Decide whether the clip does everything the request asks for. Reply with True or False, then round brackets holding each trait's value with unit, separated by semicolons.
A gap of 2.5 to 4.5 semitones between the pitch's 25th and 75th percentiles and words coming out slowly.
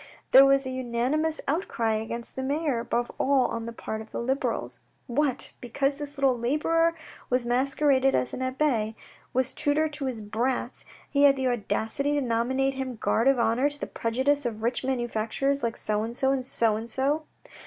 False (3.2 semitones; 190 wpm)